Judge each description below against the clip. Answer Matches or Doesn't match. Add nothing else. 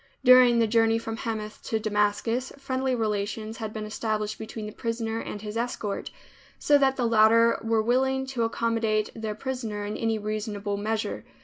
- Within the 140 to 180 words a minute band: Matches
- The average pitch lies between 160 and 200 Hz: Doesn't match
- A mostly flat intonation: Matches